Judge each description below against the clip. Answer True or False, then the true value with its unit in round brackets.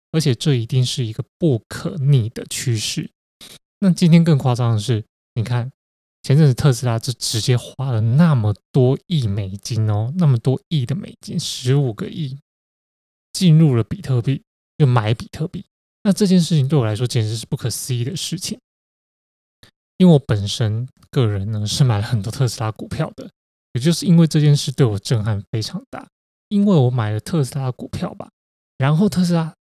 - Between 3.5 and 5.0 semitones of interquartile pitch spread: False (5.6 semitones)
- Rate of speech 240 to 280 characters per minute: True (270 characters per minute)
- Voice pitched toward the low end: True (130 Hz)